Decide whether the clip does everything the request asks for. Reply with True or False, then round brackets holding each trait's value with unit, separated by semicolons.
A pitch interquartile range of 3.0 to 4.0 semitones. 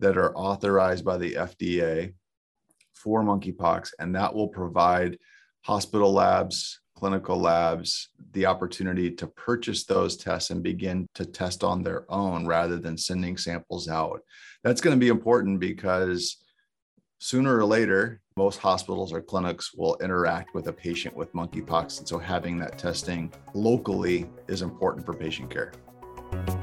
False (2.6 semitones)